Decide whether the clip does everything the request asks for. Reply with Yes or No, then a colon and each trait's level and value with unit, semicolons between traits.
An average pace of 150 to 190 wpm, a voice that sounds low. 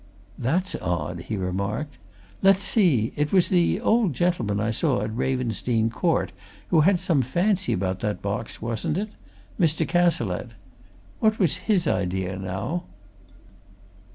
No: slow, 135 wpm; low, 130 Hz